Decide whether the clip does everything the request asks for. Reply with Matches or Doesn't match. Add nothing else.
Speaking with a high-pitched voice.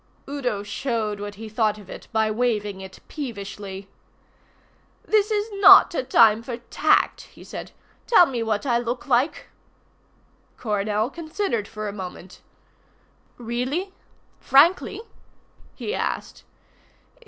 Matches